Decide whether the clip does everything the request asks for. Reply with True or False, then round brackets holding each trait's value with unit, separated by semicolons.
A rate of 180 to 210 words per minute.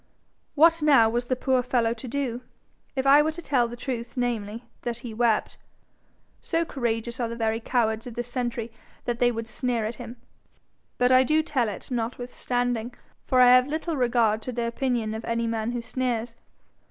True (190 wpm)